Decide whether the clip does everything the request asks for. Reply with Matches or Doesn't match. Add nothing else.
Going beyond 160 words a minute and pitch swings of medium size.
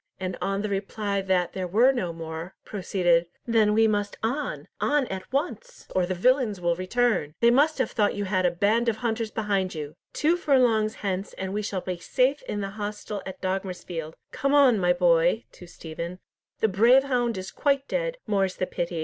Matches